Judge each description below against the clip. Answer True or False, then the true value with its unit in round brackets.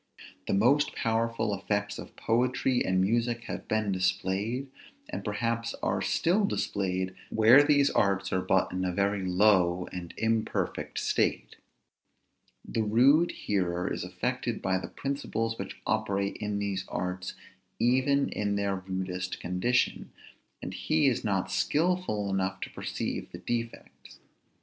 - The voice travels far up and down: False (4.0 semitones)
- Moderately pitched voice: False (105 Hz)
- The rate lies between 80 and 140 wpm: True (135 wpm)